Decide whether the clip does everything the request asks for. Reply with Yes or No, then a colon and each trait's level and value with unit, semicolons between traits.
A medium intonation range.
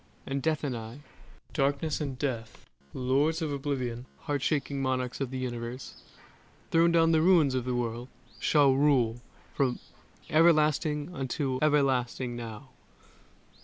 Yes: average, 3.2 semitones